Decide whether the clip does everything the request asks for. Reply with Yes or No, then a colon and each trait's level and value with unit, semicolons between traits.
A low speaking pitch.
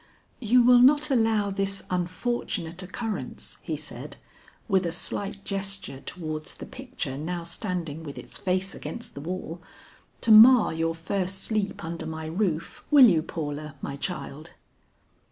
No: medium, 185 Hz